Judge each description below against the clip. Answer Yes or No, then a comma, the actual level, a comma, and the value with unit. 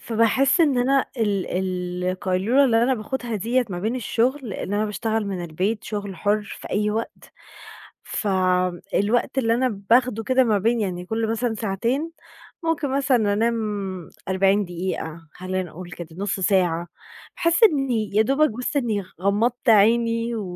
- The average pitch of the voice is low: No, high, 220 Hz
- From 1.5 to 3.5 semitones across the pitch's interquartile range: No, average, 4.2 semitones